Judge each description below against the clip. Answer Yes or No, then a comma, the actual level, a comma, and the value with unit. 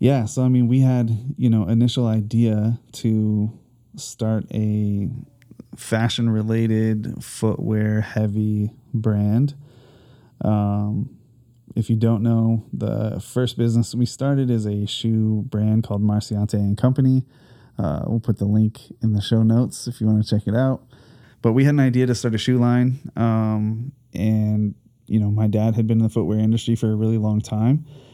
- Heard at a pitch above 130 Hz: No, low, 115 Hz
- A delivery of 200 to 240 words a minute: No, average, 170 wpm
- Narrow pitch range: Yes, narrow, 2.3 semitones